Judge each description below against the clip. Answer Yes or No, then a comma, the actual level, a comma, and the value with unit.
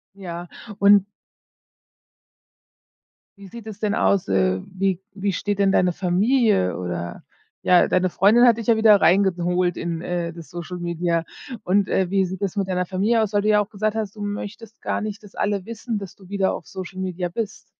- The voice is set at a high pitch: Yes, high, 195 Hz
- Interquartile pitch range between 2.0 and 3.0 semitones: Yes, average, 2.7 semitones